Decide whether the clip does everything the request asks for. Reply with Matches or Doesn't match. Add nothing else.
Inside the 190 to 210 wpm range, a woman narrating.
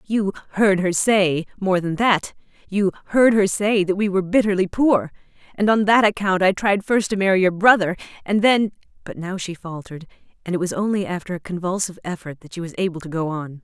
Matches